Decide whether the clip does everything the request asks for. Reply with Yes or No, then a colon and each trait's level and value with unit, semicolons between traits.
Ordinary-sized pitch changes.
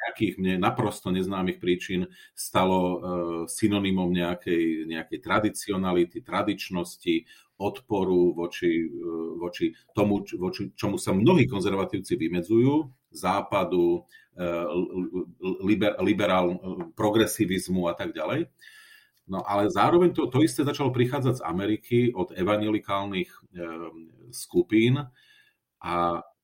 Yes: average, 4.8 semitones